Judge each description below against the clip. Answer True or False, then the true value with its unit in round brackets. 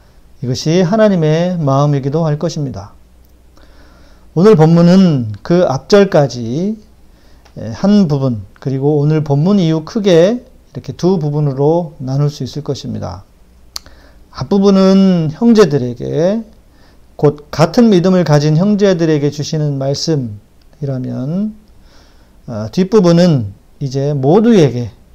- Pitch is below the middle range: False (150 Hz)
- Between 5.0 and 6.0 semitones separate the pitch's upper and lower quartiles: False (6.5 semitones)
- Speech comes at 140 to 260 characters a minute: True (235 characters per minute)